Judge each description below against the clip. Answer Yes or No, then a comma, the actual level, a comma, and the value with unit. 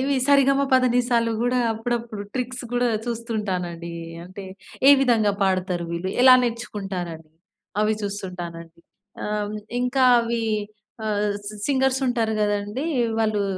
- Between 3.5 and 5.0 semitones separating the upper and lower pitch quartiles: Yes, average, 4.2 semitones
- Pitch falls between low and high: No, high, 220 Hz